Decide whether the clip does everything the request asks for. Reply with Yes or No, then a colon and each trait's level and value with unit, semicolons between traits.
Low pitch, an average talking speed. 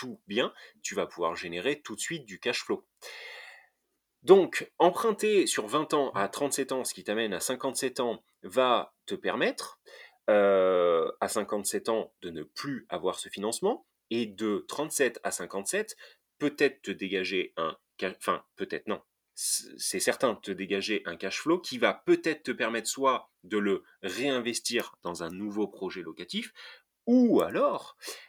Yes: low, 130 Hz; average, 155 wpm